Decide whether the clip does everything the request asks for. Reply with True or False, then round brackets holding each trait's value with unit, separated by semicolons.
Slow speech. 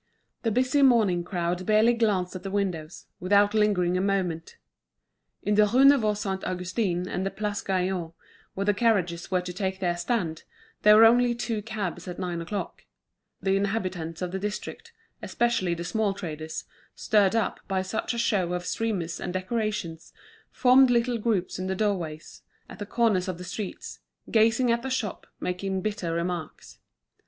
False (170 wpm)